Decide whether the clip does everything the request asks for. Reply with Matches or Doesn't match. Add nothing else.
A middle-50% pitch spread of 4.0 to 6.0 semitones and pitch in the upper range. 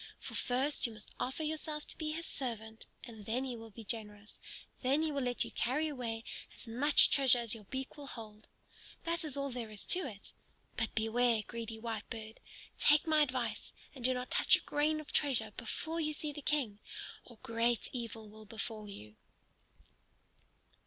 Matches